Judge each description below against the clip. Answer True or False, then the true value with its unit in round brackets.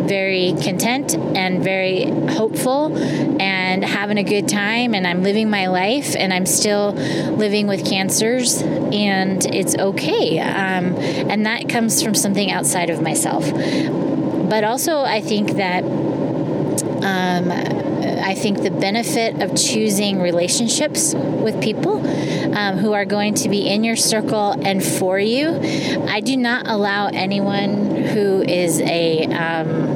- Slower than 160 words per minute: True (140 wpm)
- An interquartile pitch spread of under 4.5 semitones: True (2.8 semitones)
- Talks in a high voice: True (200 Hz)